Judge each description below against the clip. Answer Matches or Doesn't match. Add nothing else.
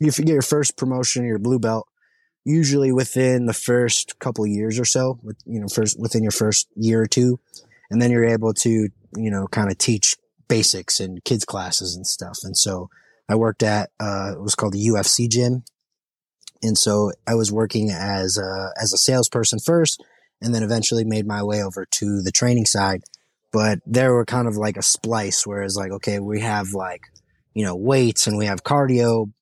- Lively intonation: Doesn't match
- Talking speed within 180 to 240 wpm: Matches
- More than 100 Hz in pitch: Matches